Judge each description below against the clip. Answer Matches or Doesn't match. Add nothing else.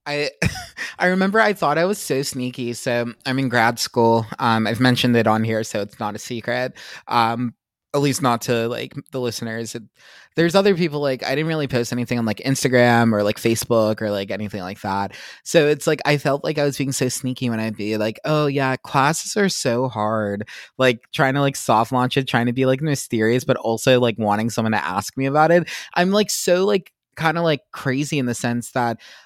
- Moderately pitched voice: Doesn't match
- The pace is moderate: Doesn't match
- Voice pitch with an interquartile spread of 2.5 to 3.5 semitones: Doesn't match